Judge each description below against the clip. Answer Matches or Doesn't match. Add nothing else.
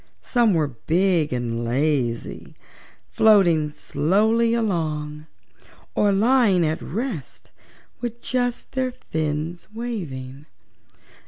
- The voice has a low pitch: Doesn't match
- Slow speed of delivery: Matches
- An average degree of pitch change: Doesn't match